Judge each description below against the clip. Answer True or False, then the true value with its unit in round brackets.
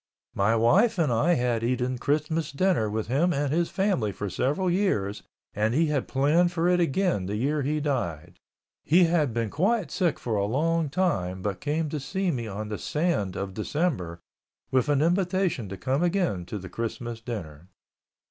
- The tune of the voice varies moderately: False (7.9 semitones)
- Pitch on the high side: False (140 Hz)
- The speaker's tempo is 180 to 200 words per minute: True (185 wpm)